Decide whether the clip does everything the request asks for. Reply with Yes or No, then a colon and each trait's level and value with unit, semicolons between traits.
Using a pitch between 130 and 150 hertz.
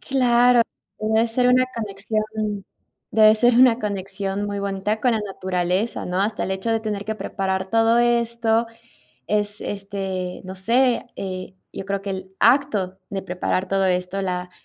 No: high, 205 Hz